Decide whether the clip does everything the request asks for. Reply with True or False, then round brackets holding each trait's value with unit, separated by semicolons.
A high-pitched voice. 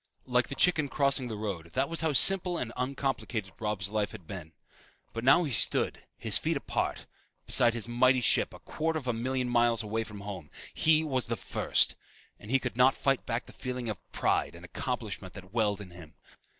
False (120 Hz)